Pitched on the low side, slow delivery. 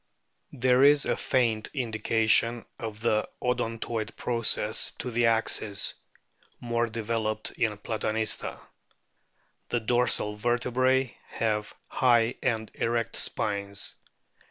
Yes: low, 115 Hz; slow, 100 wpm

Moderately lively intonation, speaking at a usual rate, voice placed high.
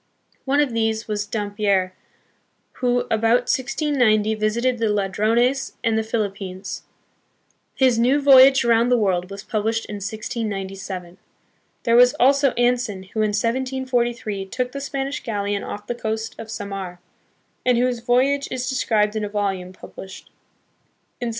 Yes: average, 3.4 semitones; average, 145 wpm; high, 225 Hz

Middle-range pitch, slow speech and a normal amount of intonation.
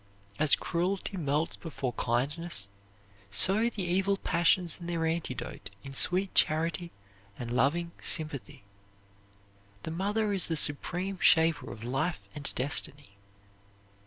Yes: medium, 165 Hz; slow, 120 wpm; average, 4.1 semitones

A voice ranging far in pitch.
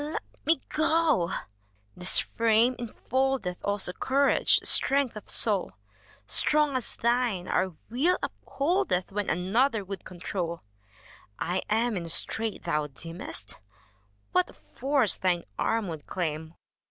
Yes: wide, 6.7 semitones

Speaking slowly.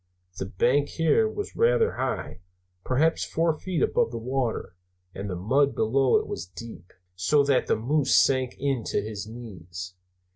No: average, 160 wpm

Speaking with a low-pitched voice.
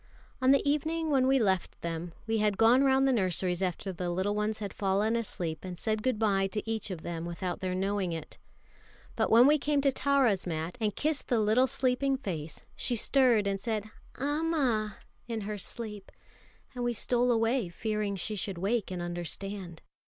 No: high, 215 Hz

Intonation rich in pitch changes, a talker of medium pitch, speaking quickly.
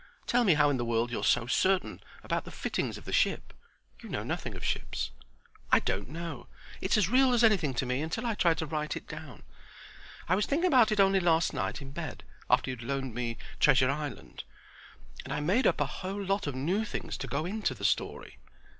Yes: wide, 6.9 semitones; medium, 160 Hz; fast, 220 wpm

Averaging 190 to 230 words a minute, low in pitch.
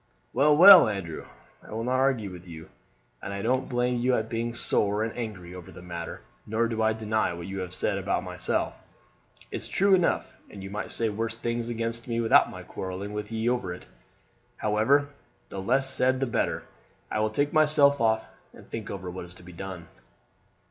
Yes: average, 195 wpm; low, 110 Hz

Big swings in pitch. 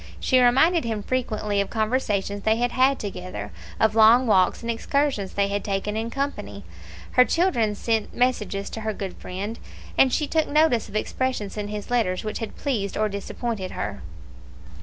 No: average, 3.8 semitones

